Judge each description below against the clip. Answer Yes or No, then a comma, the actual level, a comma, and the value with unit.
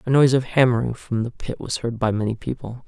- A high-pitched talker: No, low, 120 Hz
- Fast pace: Yes, fast, 250 wpm